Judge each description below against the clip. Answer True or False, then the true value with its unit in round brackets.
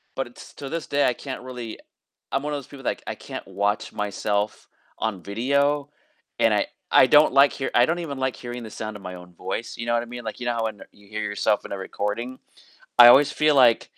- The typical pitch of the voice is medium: False (120 Hz)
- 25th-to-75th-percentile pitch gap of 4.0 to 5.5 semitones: True (4.4 semitones)